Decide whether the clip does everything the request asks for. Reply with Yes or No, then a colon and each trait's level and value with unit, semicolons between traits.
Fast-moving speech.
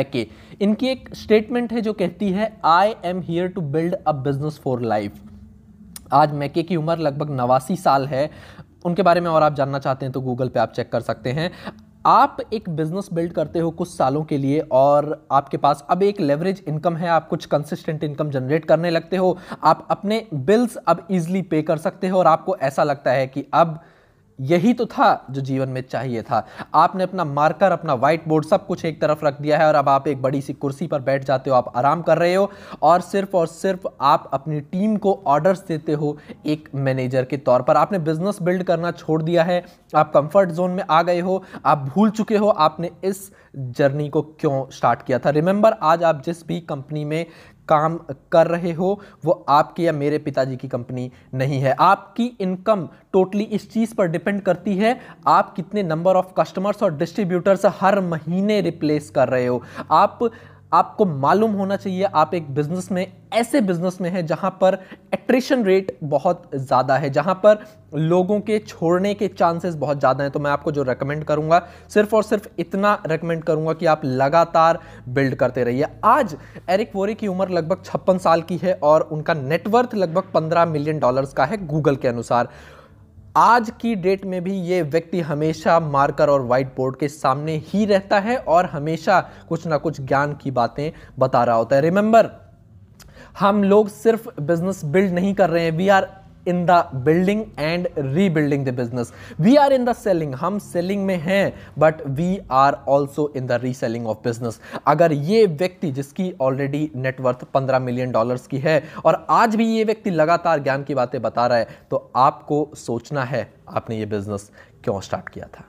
Yes: fast, 195 wpm